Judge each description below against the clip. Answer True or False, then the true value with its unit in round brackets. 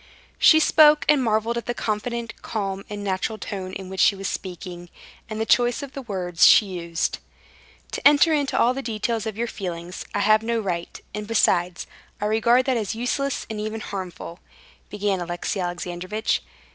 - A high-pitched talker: True (210 Hz)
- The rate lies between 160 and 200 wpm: True (180 wpm)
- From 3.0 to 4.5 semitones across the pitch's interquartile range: True (4.1 semitones)